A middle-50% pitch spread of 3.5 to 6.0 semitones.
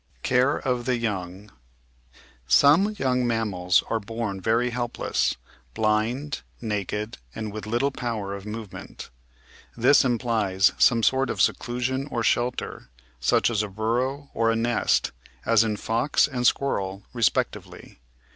No: average, 2.9 semitones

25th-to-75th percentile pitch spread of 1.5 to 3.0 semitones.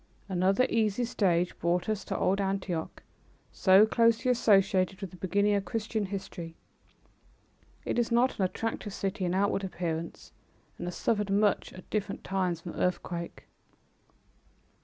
Yes: average, 2.7 semitones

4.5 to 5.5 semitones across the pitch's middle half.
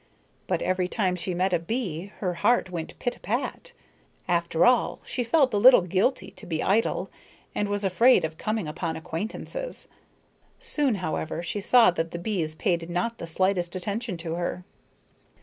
Yes: average, 4.9 semitones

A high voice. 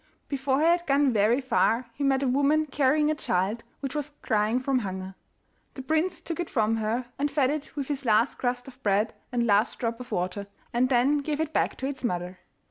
Yes: very high, 260 Hz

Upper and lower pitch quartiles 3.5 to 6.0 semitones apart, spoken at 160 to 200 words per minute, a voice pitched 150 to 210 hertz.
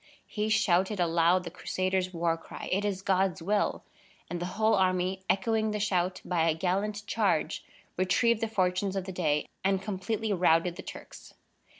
No: narrow, 2.6 semitones; average, 170 wpm; high, 190 Hz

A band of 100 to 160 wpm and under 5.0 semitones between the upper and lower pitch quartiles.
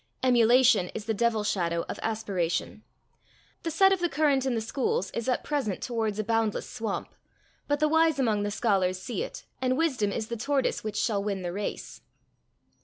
No: average, 185 wpm; average, 4.5 semitones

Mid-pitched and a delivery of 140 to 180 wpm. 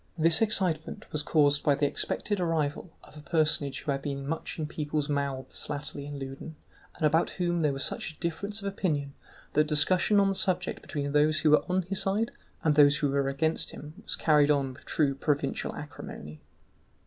No: medium, 150 Hz; average, 195 wpm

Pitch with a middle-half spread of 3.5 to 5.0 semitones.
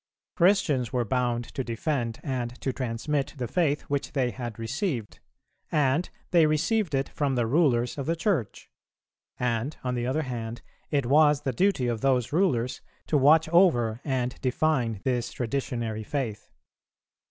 Yes: average, 4.1 semitones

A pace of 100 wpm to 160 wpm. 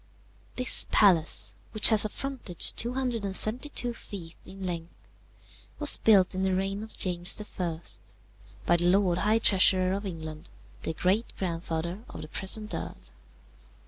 Yes: average, 140 wpm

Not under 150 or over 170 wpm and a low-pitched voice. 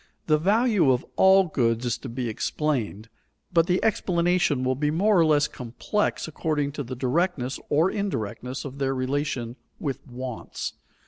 No: average, 155 wpm; medium, 145 Hz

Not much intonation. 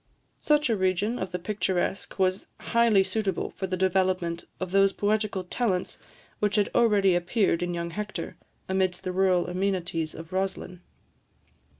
Yes: narrow, 2.3 semitones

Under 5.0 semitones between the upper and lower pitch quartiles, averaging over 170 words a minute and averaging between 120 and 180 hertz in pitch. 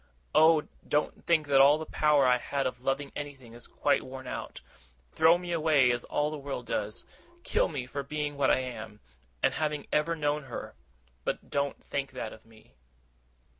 Yes: average, 2.8 semitones; average, 185 wpm; medium, 140 Hz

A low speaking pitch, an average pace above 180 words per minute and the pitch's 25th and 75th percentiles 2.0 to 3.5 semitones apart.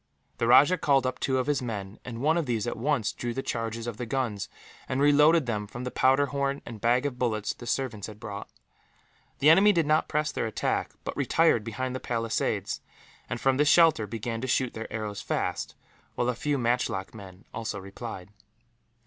No: low, 120 Hz; average, 200 wpm; average, 3.9 semitones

